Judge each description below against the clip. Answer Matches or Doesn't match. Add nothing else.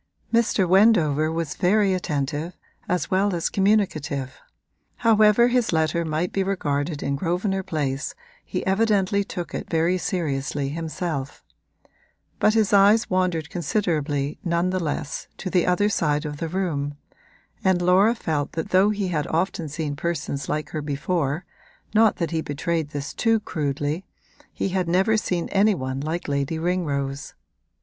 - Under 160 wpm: Matches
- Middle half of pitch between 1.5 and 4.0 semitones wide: Doesn't match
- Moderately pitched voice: Matches